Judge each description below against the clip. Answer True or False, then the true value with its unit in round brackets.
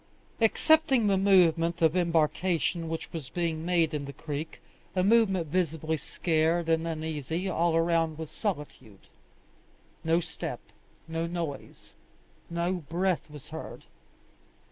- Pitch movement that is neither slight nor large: False (2.1 semitones)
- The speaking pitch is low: False (165 Hz)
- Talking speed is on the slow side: True (120 wpm)